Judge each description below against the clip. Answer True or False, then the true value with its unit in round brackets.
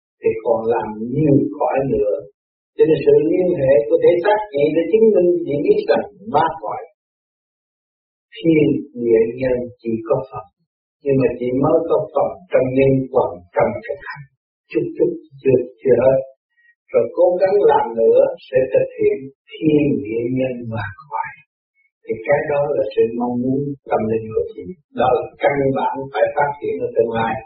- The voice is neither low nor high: True (165 Hz)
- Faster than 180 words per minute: False (175 wpm)